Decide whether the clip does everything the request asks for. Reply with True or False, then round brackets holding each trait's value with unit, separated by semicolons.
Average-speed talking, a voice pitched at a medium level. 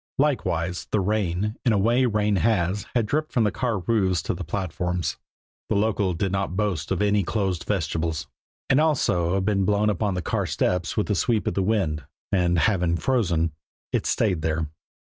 False (185 wpm; 95 Hz)